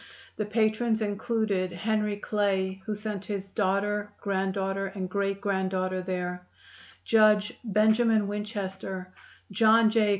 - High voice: Yes, high, 205 Hz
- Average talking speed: No, slow, 110 wpm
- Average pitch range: No, narrow, 2.1 semitones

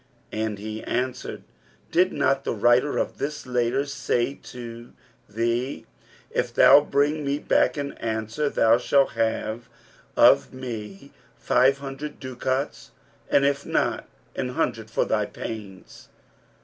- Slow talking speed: Yes, slow, 130 wpm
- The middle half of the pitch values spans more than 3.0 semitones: Yes, average, 3.8 semitones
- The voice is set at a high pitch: No, low, 125 Hz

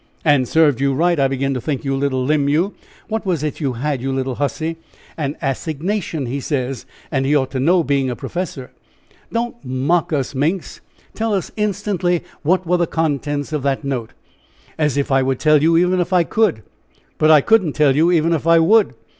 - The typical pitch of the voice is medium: Yes, medium, 150 Hz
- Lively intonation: No, average, 4.2 semitones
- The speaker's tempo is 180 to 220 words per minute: Yes, fast, 205 wpm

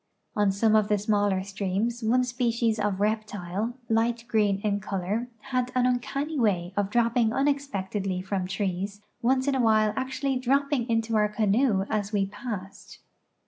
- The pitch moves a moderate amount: Yes, average, 3.4 semitones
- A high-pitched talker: Yes, high, 215 Hz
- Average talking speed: Yes, average, 150 wpm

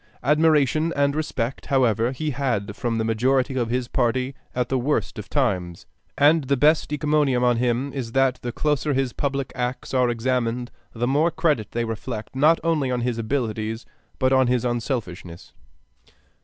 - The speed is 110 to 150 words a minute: No, average, 170 wpm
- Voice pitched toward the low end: Yes, low, 130 Hz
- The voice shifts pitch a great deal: No, average, 3.2 semitones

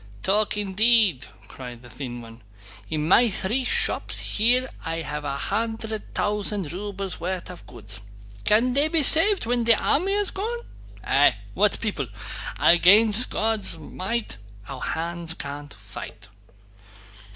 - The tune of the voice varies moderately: No, wide, 7.4 semitones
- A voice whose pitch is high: Yes, high, 200 Hz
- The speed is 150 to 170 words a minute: No, slow, 135 wpm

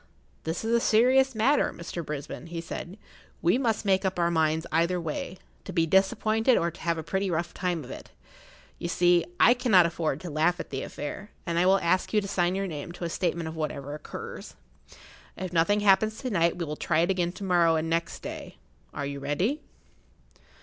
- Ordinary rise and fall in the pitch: Yes, average, 3.1 semitones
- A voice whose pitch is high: No, medium, 175 Hz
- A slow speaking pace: No, fast, 205 wpm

